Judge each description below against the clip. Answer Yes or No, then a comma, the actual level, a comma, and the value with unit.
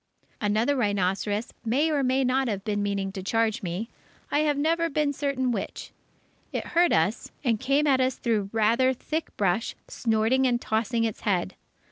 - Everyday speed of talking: Yes, average, 170 wpm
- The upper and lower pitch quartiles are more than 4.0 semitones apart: Yes, average, 4.6 semitones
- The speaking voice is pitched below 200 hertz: No, high, 230 Hz